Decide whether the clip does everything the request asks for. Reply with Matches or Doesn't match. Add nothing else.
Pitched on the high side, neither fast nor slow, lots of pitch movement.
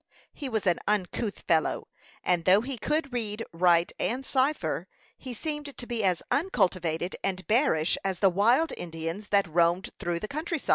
Matches